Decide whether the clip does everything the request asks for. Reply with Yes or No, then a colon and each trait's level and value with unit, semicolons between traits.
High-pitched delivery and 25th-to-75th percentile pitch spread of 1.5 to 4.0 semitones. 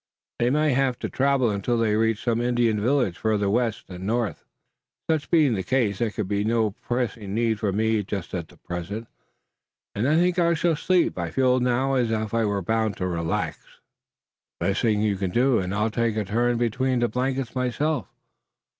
No: low, 115 Hz; average, 3.6 semitones